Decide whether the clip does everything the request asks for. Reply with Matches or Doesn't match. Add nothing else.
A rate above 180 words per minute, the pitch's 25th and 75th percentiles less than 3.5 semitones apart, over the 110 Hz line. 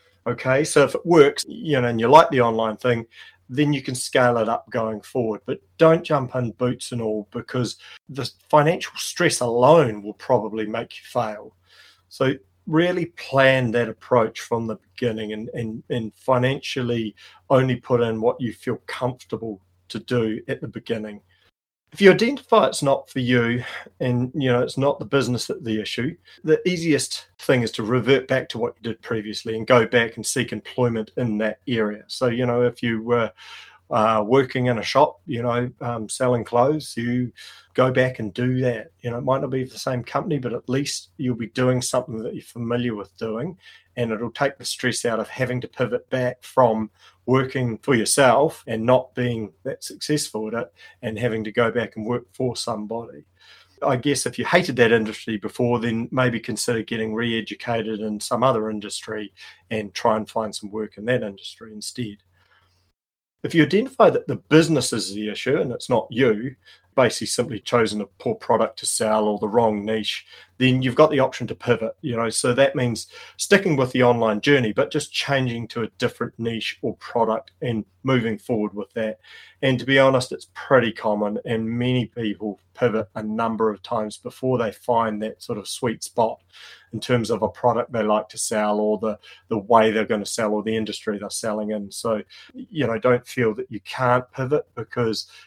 Matches